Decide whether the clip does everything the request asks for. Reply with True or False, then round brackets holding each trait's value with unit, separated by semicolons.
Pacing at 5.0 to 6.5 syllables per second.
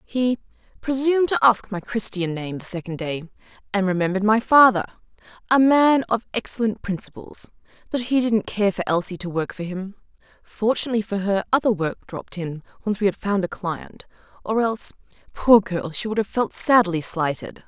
True (5.4 syllables/s)